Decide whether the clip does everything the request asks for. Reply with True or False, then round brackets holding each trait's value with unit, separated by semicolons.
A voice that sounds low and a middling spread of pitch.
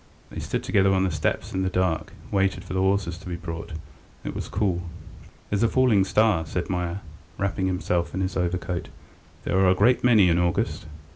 False (95 Hz; 2.0 semitones)